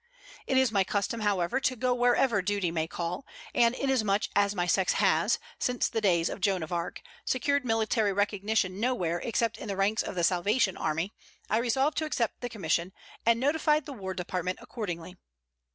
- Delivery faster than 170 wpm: Yes, average, 185 wpm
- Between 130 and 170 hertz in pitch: No, high, 205 Hz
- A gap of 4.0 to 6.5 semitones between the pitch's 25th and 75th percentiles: Yes, average, 5.0 semitones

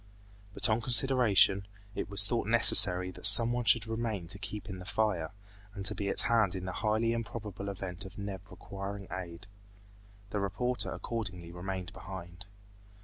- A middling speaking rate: Yes, average, 160 wpm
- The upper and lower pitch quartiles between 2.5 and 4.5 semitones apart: Yes, average, 3.3 semitones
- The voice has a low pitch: Yes, low, 100 Hz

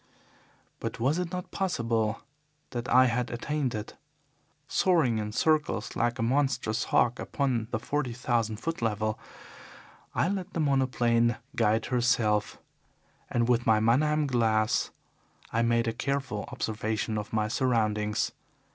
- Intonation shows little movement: No, average, 3.3 semitones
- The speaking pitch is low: Yes, low, 120 Hz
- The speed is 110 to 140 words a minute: Yes, slow, 135 wpm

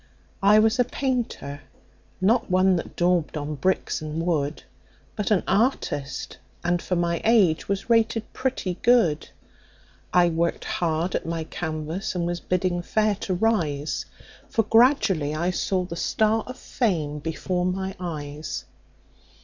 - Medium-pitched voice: Yes, medium, 180 Hz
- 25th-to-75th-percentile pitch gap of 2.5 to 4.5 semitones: No, average, 5.0 semitones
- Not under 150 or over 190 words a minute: No, average, 140 wpm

